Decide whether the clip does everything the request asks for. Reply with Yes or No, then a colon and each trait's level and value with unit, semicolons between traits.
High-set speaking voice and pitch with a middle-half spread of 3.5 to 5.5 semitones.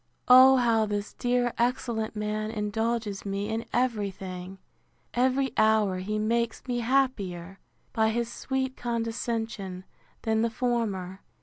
No: high, 225 Hz; average, 2.8 semitones